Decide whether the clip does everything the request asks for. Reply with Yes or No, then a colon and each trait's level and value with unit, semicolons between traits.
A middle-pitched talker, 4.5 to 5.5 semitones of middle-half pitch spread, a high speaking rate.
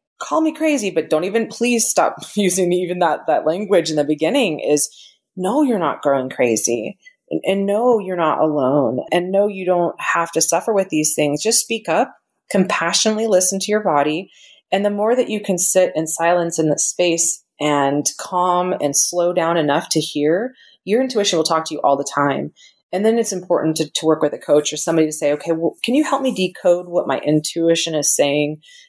Yes: medium, 175 Hz; average, 5.0 semitones; fast, 210 wpm